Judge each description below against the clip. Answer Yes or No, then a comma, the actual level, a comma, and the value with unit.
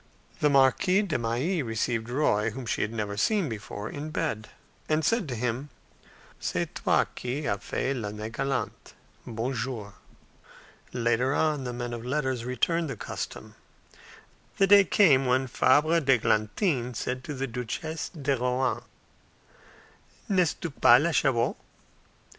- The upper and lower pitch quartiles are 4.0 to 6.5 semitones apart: Yes, average, 4.4 semitones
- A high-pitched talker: No, low, 130 Hz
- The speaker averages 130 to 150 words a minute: Yes, average, 140 wpm